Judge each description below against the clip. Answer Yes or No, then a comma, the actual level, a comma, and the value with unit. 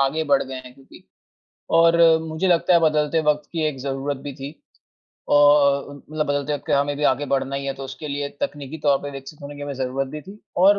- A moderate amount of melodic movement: No, narrow, 2.0 semitones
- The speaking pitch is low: No, medium, 145 Hz